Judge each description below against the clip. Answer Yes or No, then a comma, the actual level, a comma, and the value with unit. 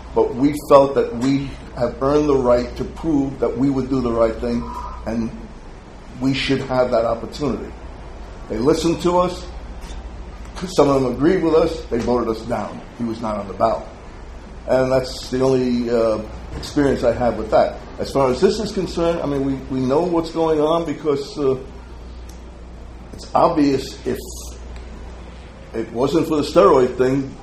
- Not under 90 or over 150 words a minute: No, average, 175 wpm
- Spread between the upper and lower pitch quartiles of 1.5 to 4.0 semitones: No, average, 4.6 semitones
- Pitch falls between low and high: No, low, 130 Hz